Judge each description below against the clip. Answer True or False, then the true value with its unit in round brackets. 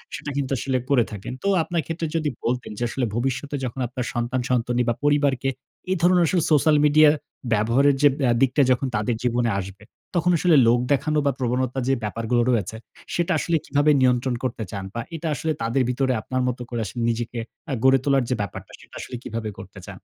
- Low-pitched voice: True (130 Hz)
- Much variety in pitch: False (3.3 semitones)